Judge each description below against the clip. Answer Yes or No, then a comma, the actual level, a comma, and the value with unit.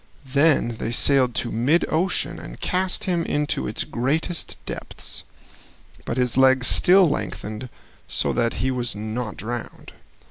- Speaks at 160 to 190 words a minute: No, average, 140 wpm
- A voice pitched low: Yes, low, 130 Hz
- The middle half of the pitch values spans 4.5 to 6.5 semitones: Yes, average, 5.1 semitones